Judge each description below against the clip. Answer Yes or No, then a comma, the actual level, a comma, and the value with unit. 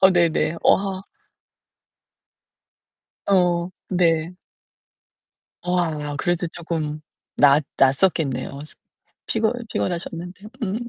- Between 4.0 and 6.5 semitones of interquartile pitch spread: No, average, 3.2 semitones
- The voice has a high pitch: No, medium, 170 Hz